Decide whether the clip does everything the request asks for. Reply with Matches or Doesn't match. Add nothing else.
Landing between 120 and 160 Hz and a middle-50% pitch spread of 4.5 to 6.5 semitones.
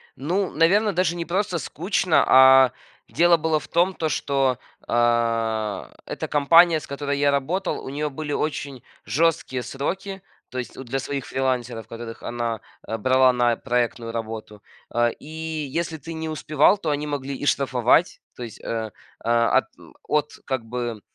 Matches